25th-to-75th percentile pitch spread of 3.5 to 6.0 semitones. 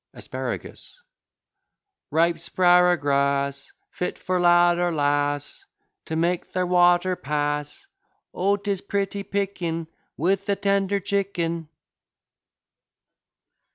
Yes: average, 3.8 semitones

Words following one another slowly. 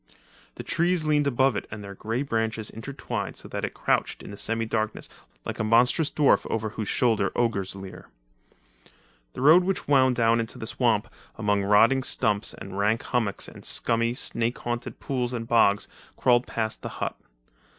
No: average, 170 wpm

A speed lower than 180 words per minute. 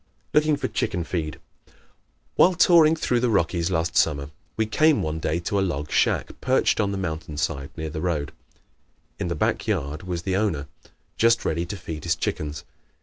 No: average, 190 wpm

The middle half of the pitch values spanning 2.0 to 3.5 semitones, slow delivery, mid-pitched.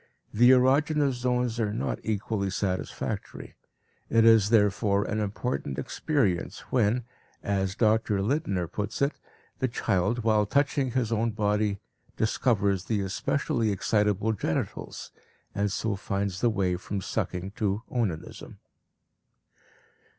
No: average, 3.2 semitones; slow, 120 wpm; low, 105 Hz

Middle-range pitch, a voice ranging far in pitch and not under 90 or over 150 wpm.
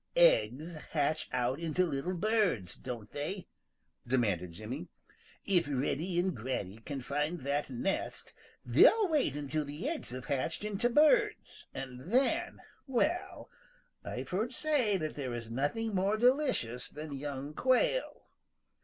Yes: medium, 155 Hz; wide, 8.9 semitones; slow, 135 wpm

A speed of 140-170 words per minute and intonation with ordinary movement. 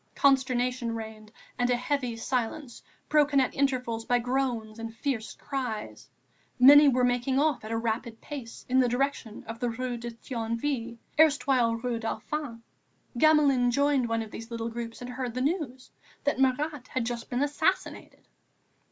Yes: average, 155 wpm; average, 3.0 semitones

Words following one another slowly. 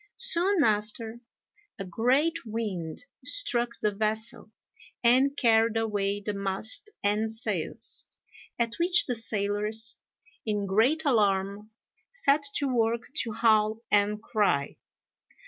Yes: slow, 110 wpm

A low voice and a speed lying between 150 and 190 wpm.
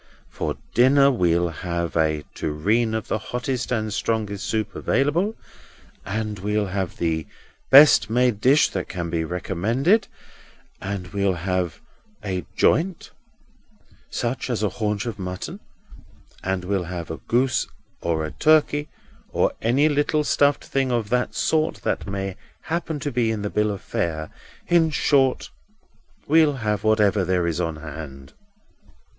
No: low, 105 Hz; average, 140 wpm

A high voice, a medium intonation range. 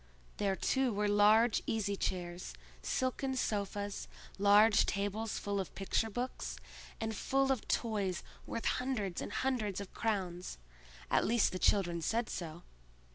Yes: high, 205 Hz; average, 3.3 semitones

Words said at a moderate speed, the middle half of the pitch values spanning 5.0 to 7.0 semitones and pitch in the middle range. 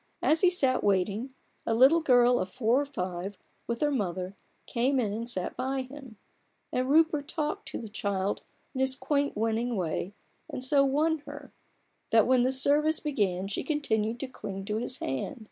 No: average, 180 wpm; average, 5.3 semitones; very high, 250 Hz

